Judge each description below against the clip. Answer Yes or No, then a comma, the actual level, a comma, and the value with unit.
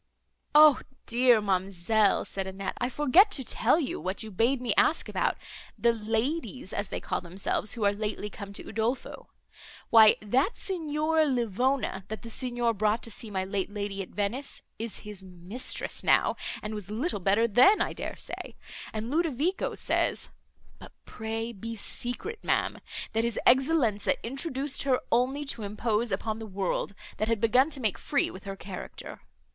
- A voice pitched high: Yes, high, 225 Hz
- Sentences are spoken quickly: No, average, 170 wpm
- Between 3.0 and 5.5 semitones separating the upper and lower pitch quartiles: Yes, average, 4.2 semitones